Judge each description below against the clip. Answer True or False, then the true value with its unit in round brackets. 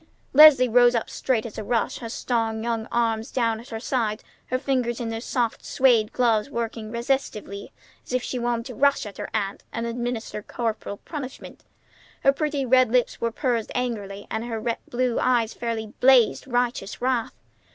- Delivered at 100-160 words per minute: False (175 wpm)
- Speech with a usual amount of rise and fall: False (2.2 semitones)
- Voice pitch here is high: True (235 Hz)